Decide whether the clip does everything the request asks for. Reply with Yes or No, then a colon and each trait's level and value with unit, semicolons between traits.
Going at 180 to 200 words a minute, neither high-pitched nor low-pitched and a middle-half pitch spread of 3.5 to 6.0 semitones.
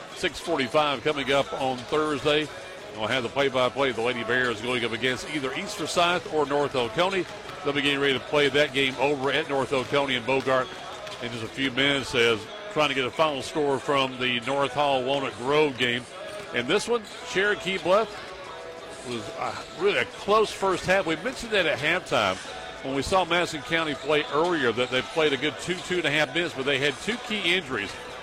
Yes: average, 195 wpm; medium, 145 Hz; average, 4.0 semitones